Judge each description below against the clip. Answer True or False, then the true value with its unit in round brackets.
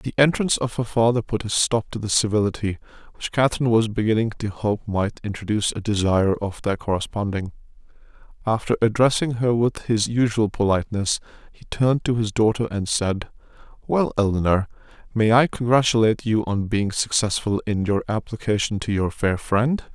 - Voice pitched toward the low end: True (110 Hz)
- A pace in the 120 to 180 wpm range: True (160 wpm)